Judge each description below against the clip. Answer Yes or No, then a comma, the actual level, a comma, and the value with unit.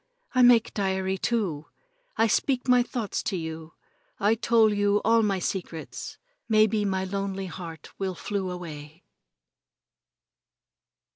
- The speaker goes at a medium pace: No, slow, 125 wpm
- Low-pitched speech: No, high, 195 Hz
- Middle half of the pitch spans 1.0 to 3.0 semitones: No, average, 3.5 semitones